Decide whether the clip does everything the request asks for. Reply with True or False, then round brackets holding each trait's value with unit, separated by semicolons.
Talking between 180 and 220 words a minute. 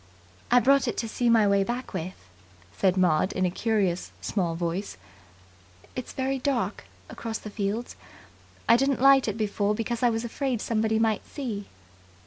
False (165 wpm)